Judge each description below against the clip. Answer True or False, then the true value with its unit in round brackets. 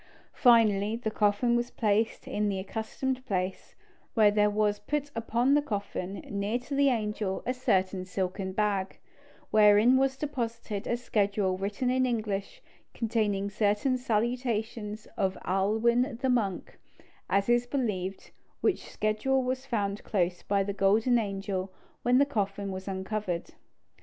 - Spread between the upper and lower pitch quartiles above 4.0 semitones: False (3.5 semitones)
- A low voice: False (215 Hz)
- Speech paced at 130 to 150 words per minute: True (140 wpm)